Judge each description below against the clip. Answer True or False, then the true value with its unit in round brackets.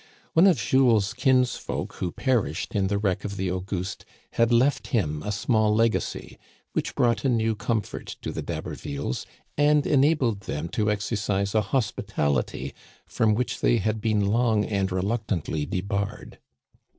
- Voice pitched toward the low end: True (105 Hz)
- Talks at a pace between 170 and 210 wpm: False (150 wpm)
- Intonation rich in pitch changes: False (3.5 semitones)